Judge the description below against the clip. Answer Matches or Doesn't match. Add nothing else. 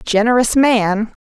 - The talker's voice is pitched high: Matches